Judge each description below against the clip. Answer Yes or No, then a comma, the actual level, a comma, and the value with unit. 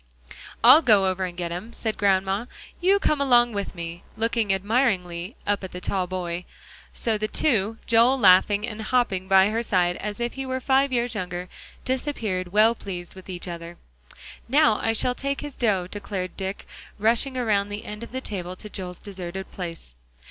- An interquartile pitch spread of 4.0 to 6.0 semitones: Yes, average, 4.3 semitones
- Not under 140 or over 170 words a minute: No, average, 185 wpm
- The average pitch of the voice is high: Yes, high, 205 Hz